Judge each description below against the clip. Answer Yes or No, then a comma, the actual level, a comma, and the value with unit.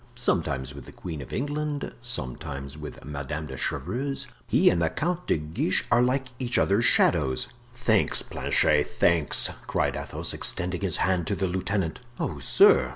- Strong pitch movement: Yes, wide, 8.4 semitones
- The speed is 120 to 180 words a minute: Yes, average, 160 wpm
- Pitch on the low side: Yes, very low, 90 Hz